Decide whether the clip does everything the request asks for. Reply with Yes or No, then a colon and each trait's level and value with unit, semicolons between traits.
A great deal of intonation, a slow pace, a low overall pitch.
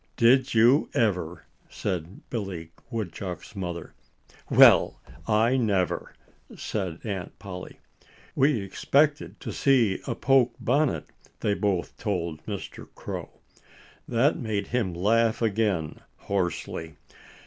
No: average, 4.5 semitones; slow, 105 wpm; low, 105 Hz